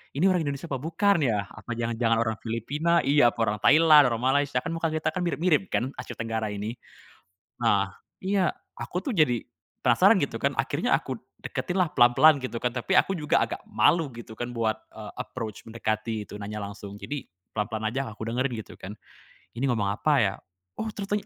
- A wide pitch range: Yes, wide, 5.9 semitones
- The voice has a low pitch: Yes, low, 125 Hz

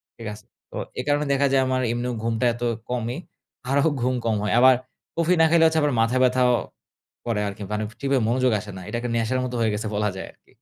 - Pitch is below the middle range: Yes, low, 125 Hz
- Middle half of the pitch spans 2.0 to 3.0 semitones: Yes, narrow, 2.6 semitones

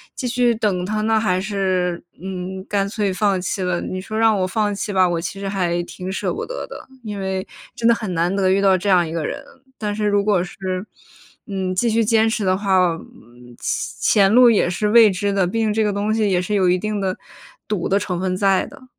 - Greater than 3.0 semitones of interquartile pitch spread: No, narrow, 2.5 semitones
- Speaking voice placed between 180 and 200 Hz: Yes, high, 195 Hz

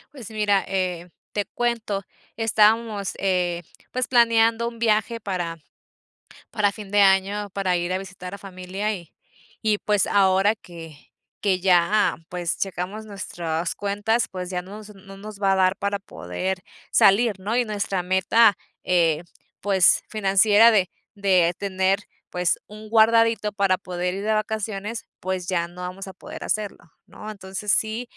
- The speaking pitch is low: No, high, 195 Hz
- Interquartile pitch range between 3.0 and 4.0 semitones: No, narrow, 2.6 semitones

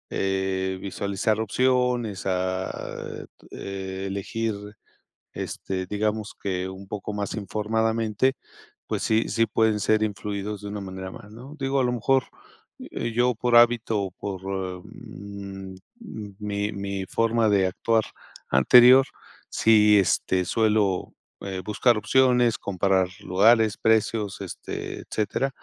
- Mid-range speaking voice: No, low, 105 Hz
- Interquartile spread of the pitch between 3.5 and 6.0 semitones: No, average, 2.8 semitones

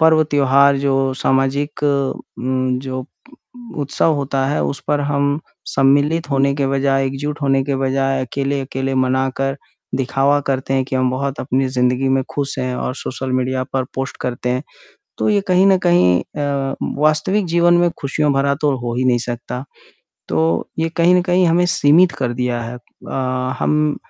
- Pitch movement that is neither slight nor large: No, narrow, 2.0 semitones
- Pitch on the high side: No, low, 135 Hz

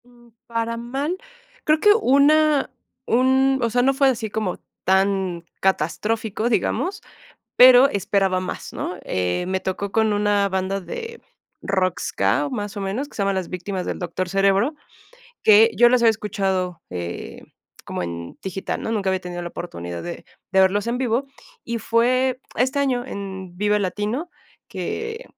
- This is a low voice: No, high, 205 Hz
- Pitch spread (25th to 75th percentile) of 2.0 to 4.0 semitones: No, average, 4.9 semitones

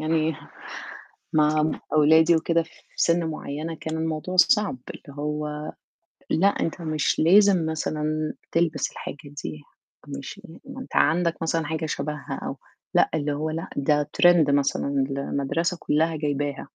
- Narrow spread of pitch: Yes, narrow, 1.8 semitones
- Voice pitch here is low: No, medium, 155 Hz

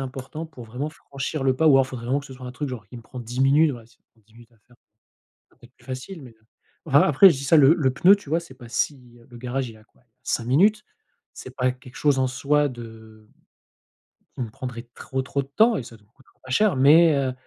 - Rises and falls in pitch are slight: No, average, 3.0 semitones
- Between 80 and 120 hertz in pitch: No, low, 130 Hz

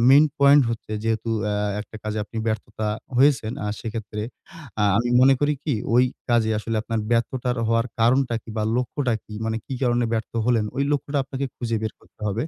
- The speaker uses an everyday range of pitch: Yes, average, 3.0 semitones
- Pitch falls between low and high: No, low, 115 Hz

